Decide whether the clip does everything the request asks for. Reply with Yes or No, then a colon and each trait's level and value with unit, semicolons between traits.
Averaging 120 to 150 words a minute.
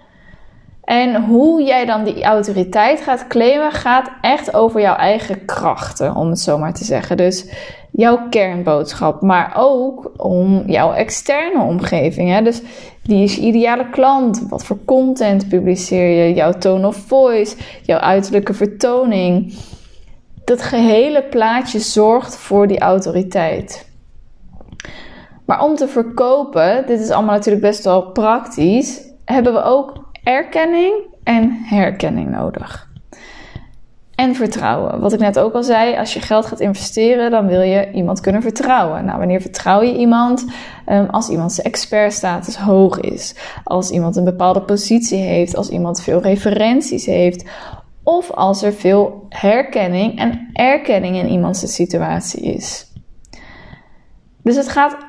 Yes: average, 140 wpm